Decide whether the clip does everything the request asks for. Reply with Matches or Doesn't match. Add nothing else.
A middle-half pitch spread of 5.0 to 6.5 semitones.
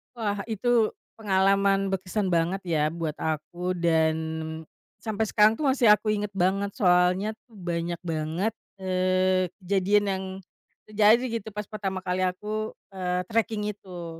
Doesn't match